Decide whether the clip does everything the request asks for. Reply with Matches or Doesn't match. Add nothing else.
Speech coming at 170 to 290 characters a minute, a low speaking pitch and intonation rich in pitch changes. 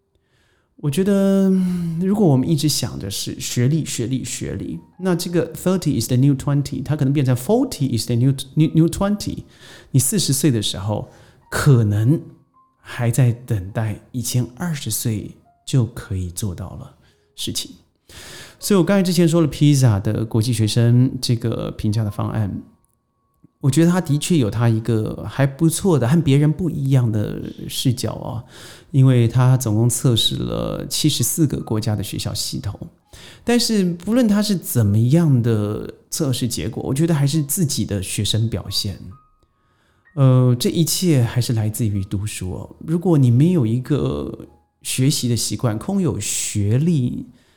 Matches